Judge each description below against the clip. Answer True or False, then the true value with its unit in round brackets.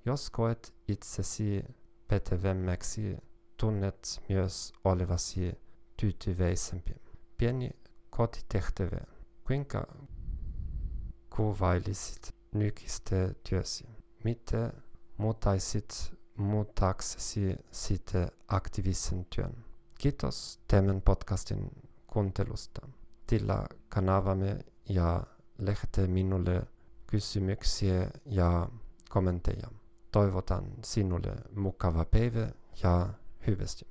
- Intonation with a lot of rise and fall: False (3.8 semitones)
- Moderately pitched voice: False (100 Hz)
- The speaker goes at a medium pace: False (65 wpm)